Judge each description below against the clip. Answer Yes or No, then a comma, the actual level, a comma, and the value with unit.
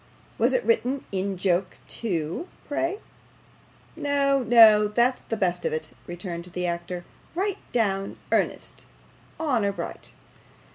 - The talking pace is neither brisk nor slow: No, slow, 125 wpm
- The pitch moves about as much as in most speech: No, wide, 7.4 semitones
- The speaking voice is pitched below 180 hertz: No, high, 210 Hz